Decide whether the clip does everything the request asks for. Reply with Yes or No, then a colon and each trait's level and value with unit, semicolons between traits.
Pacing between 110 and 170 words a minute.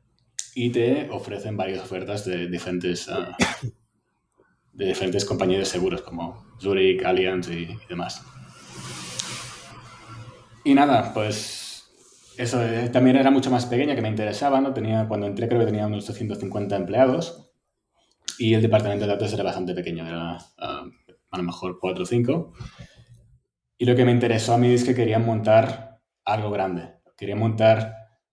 Yes: average, 155 wpm